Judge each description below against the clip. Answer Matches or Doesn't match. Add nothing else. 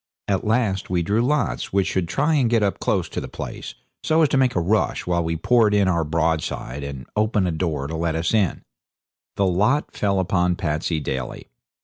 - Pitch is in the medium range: Doesn't match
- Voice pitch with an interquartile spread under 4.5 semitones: Doesn't match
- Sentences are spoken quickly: Matches